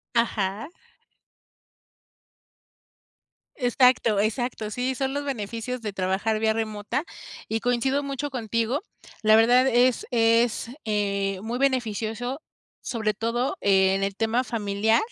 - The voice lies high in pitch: Yes, high, 230 Hz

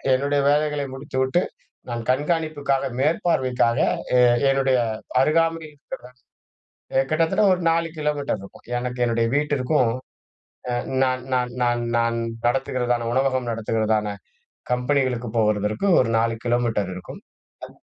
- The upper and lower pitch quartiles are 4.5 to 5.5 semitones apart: No, average, 3.8 semitones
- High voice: No, low, 130 Hz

